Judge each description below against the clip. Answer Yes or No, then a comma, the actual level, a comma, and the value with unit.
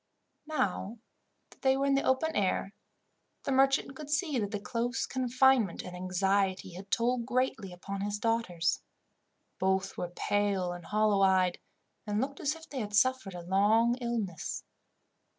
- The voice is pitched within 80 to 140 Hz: No, high, 210 Hz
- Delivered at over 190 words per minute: No, average, 155 wpm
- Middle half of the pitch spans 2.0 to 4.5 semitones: No, average, 5.3 semitones